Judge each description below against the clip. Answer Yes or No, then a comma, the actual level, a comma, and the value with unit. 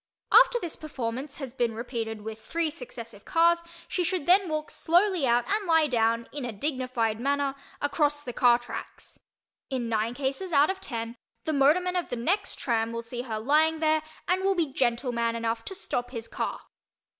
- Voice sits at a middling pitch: No, very high, 270 Hz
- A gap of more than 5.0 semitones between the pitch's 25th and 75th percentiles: Yes, wide, 5.6 semitones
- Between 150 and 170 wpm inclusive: No, average, 185 wpm